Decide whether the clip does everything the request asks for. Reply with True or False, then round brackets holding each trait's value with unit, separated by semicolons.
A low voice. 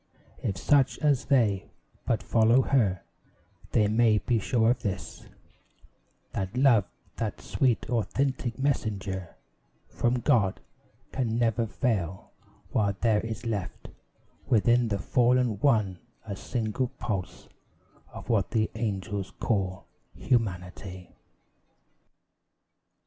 True (110 Hz)